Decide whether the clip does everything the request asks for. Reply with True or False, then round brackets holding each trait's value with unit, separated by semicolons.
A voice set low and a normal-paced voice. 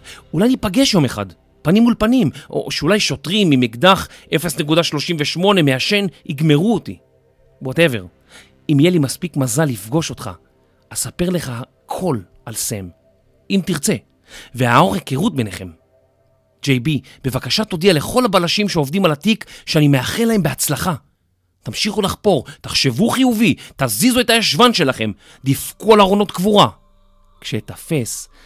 False (150 Hz; 125 wpm)